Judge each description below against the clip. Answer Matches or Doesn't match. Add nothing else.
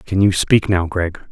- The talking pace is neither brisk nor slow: Doesn't match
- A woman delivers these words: Doesn't match